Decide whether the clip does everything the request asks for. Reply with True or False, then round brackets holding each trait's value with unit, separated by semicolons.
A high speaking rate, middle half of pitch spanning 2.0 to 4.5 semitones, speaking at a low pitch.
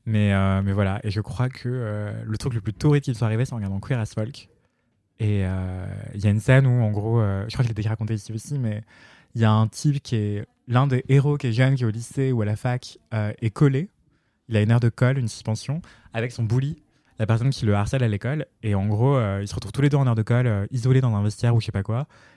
True (300 wpm; 3.4 semitones; 115 Hz)